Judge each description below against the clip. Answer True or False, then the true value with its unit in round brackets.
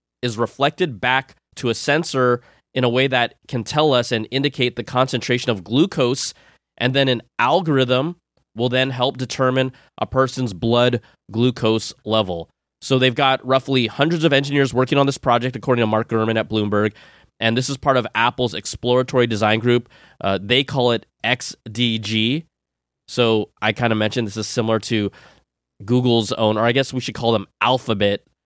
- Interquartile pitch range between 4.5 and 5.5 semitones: False (2.9 semitones)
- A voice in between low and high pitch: False (125 Hz)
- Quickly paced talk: False (175 wpm)